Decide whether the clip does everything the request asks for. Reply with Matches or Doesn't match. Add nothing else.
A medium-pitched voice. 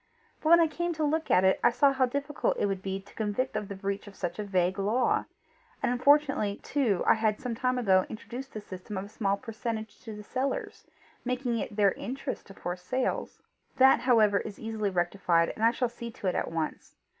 Doesn't match